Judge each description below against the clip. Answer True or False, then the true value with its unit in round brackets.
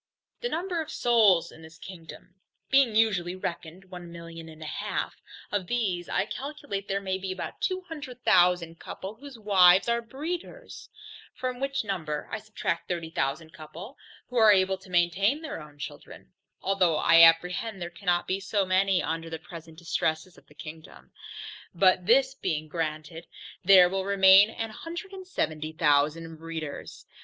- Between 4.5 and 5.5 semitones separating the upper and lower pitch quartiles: True (5.1 semitones)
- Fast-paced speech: False (165 wpm)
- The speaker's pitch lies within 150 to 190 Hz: True (185 Hz)